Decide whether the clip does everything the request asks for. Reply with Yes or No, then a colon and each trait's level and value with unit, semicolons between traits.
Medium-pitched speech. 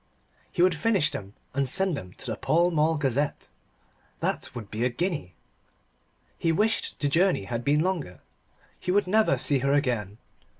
Yes: medium, 150 Hz